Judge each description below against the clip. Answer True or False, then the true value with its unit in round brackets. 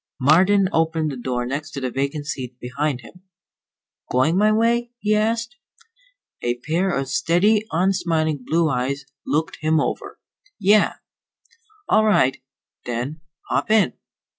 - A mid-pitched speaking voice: True (155 Hz)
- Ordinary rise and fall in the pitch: False (6.5 semitones)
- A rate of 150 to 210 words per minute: False (135 wpm)